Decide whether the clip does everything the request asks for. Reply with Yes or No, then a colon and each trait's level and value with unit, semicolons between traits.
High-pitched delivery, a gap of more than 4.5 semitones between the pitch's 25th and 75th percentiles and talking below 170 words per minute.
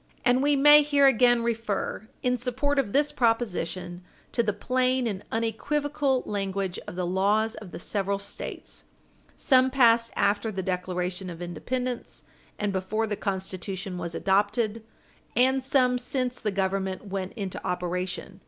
Yes: high, 215 Hz; average, 4.9 semitones; average, 145 wpm